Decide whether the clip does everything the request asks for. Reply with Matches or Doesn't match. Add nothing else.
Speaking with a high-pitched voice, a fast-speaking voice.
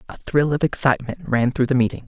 Doesn't match